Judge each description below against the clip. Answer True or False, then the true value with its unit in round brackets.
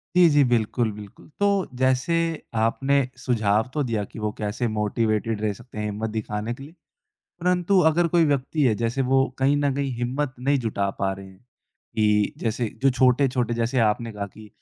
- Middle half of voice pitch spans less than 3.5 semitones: False (4.2 semitones)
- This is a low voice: True (120 Hz)